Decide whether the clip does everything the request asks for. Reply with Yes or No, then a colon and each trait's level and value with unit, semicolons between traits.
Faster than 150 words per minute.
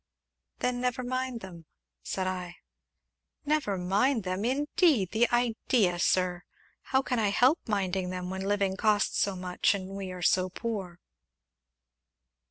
No: slow, 135 wpm